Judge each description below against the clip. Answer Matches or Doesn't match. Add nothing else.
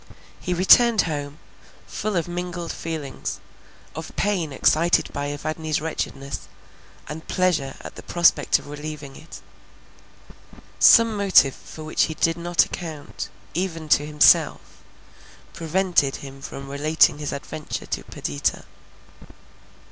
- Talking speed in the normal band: Doesn't match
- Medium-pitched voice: Matches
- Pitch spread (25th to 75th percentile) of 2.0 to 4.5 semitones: Matches